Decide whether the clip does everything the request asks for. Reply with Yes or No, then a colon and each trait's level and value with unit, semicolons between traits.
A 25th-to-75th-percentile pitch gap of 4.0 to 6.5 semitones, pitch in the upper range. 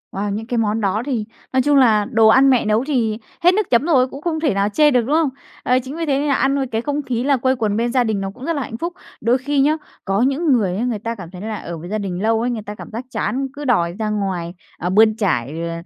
Yes: average, 4.5 semitones; high, 235 Hz